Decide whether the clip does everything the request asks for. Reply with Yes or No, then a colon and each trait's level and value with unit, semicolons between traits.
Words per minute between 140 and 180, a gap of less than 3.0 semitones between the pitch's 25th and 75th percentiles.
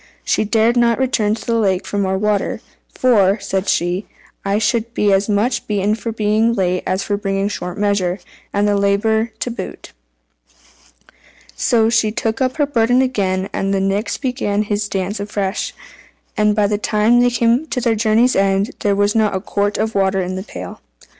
No: average, 190 wpm; narrow, 2.5 semitones